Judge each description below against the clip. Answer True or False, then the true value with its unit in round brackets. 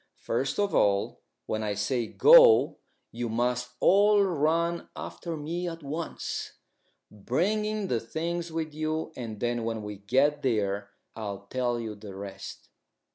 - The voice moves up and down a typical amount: False (7.5 semitones)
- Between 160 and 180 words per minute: False (140 wpm)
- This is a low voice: True (130 Hz)